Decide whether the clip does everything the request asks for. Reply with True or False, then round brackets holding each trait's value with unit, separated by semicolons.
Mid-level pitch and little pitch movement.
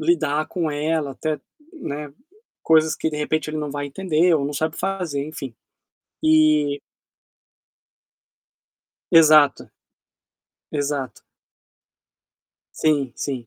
True (155 Hz; 1.7 semitones)